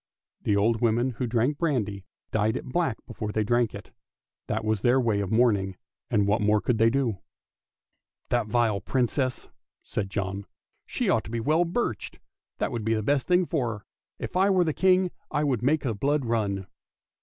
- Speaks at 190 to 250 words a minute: Yes, average, 200 wpm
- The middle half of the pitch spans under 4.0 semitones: No, average, 4.5 semitones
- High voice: No, low, 115 Hz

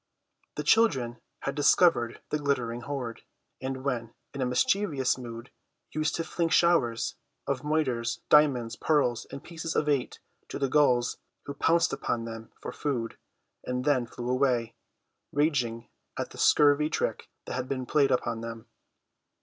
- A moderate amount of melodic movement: Yes, average, 3.8 semitones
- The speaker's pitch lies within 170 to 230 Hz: No, low, 130 Hz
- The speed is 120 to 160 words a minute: Yes, average, 150 wpm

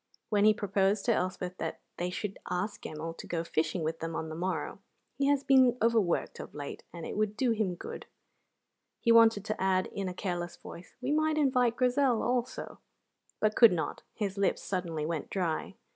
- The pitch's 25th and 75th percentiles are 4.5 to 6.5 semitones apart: Yes, average, 5.0 semitones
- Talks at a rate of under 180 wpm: No, average, 190 wpm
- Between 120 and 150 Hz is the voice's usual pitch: No, high, 200 Hz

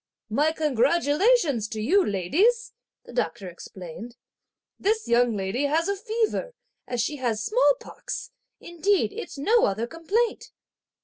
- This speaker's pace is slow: Yes, slow, 125 wpm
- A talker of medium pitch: No, very high, 295 Hz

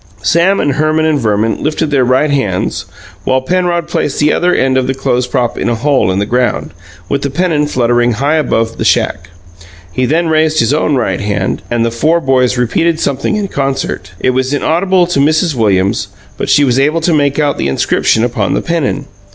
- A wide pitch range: No, average, 4.4 semitones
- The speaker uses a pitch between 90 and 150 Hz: Yes, medium, 140 Hz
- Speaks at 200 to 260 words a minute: Yes, fast, 205 wpm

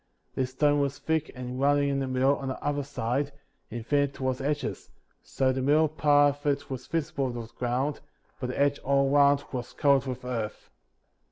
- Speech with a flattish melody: Yes, narrow, 1.9 semitones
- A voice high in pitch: No, medium, 140 Hz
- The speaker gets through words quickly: Yes, fast, 210 wpm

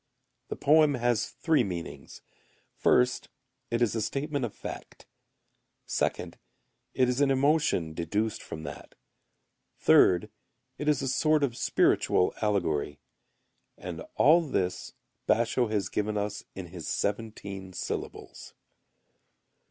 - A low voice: Yes, low, 115 Hz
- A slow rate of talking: Yes, slow, 120 wpm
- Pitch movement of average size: No, wide, 6.1 semitones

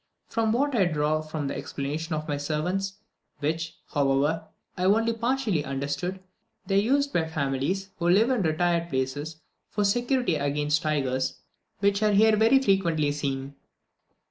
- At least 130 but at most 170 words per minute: Yes, average, 160 wpm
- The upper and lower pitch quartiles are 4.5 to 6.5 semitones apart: Yes, wide, 5.6 semitones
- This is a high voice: No, medium, 165 Hz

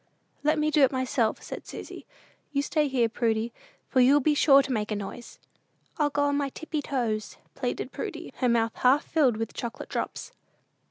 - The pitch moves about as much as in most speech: Yes, average, 3.9 semitones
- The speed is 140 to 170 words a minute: No, average, 185 wpm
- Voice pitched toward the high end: Yes, very high, 265 Hz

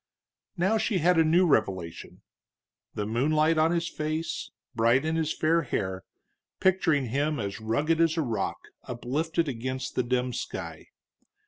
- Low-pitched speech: No, medium, 150 Hz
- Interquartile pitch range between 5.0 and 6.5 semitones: Yes, wide, 5.4 semitones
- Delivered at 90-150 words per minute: Yes, average, 145 wpm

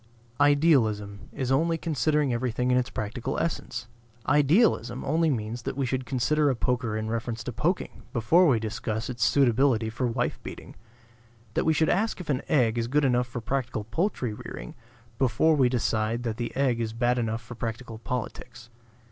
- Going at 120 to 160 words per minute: No, average, 175 wpm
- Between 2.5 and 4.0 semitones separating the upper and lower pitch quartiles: Yes, average, 3.7 semitones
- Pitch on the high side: No, low, 125 Hz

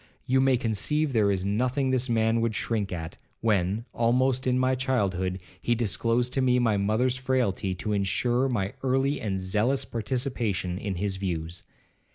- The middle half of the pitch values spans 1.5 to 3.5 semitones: No, average, 4.5 semitones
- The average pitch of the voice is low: Yes, low, 115 Hz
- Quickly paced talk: No, average, 165 wpm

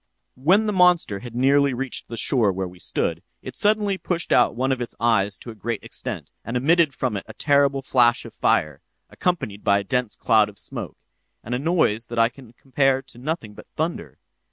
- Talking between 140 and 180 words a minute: No, fast, 205 wpm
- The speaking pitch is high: No, low, 125 Hz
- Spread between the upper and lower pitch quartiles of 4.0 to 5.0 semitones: Yes, average, 4.5 semitones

